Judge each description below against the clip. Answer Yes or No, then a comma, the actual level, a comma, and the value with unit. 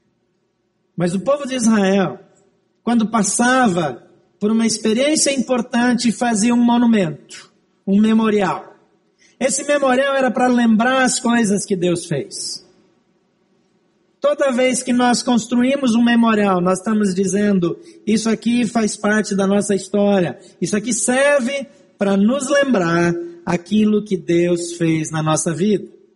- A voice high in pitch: Yes, high, 205 Hz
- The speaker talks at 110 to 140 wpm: Yes, average, 130 wpm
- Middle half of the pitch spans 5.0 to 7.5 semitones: No, average, 4.4 semitones